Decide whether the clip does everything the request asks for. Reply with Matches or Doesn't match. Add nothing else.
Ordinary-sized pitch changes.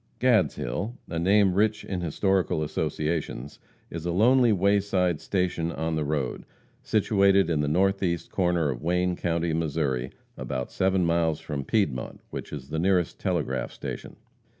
Matches